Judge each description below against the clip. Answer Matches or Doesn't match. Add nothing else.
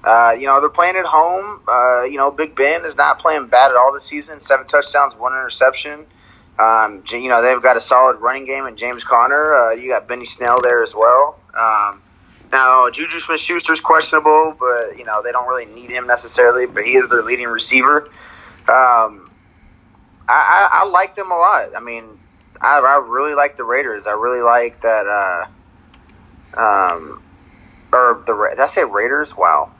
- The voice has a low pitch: Matches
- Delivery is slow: Doesn't match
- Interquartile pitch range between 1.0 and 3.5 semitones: Doesn't match